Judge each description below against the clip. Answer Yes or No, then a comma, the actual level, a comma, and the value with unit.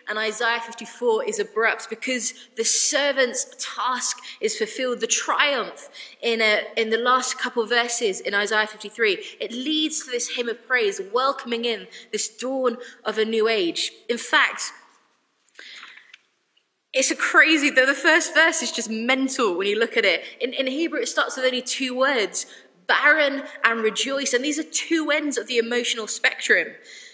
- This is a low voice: No, very high, 255 Hz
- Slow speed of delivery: No, average, 175 wpm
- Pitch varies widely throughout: No, average, 4.5 semitones